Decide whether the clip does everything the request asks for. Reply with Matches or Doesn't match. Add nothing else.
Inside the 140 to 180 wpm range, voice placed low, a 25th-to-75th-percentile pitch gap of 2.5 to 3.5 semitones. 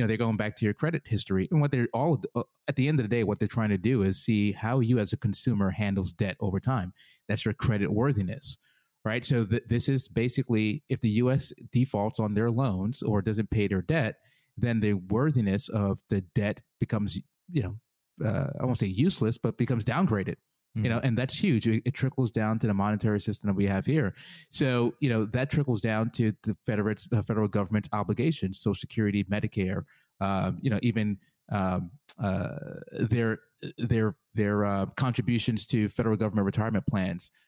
Doesn't match